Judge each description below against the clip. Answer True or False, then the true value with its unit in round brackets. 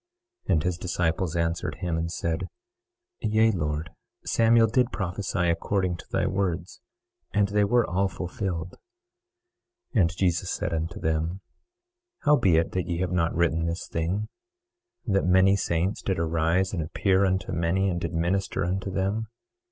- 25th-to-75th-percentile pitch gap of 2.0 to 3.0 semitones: True (2.6 semitones)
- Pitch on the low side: True (90 Hz)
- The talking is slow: False (160 wpm)